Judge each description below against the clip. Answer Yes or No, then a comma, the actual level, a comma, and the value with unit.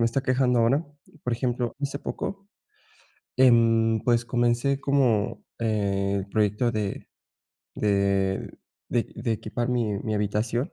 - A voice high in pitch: No, low, 115 Hz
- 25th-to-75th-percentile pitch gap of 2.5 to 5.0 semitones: Yes, average, 2.9 semitones